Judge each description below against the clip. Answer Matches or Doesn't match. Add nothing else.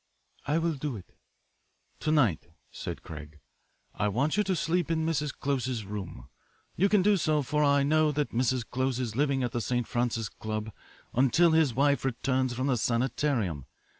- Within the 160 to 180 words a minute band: Matches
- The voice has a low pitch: Matches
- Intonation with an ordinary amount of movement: Matches